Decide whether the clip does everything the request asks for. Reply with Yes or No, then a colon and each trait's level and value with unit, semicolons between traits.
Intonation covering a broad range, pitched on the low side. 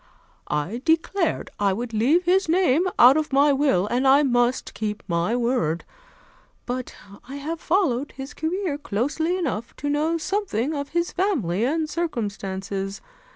No: wide, 6.4 semitones; very high, 275 Hz